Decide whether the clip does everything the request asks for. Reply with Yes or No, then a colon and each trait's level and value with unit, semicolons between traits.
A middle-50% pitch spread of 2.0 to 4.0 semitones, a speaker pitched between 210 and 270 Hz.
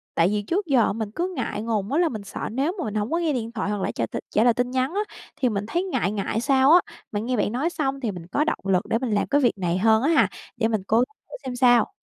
No: average, 5.1 semitones; high, 235 Hz